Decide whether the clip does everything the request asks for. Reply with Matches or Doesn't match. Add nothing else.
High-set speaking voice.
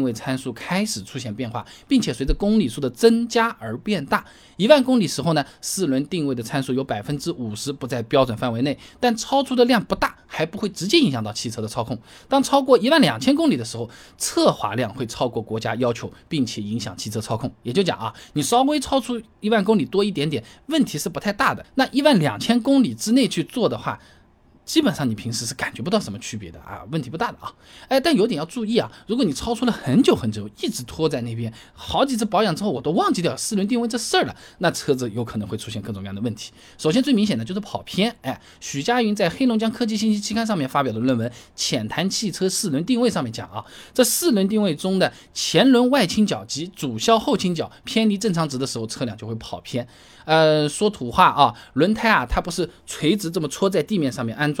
Doesn't match